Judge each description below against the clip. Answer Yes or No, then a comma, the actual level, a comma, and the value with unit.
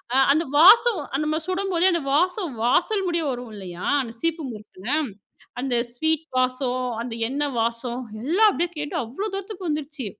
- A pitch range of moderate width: No, wide, 6.2 semitones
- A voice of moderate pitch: No, very high, 300 Hz